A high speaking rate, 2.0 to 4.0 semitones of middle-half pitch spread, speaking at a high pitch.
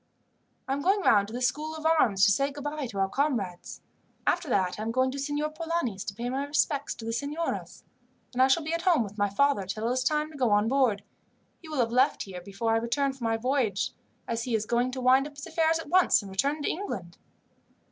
No: fast, 245 wpm; average, 5.3 semitones; very high, 260 Hz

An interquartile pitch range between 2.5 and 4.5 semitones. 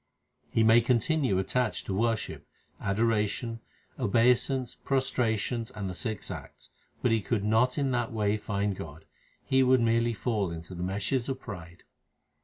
Yes: average, 3.7 semitones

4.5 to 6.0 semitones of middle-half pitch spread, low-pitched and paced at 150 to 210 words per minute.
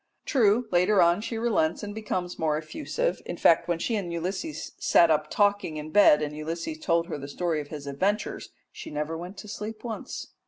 No: average, 5.1 semitones; medium, 175 Hz; average, 200 wpm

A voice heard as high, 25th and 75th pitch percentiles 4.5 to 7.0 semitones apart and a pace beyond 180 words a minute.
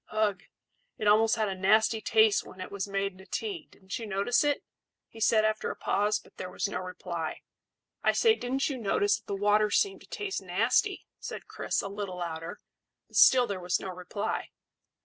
No: high, 205 Hz; average, 2.8 semitones; average, 200 wpm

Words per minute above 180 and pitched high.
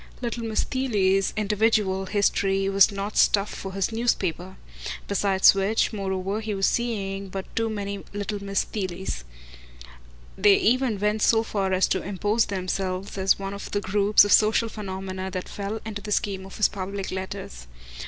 No: average, 165 wpm; high, 200 Hz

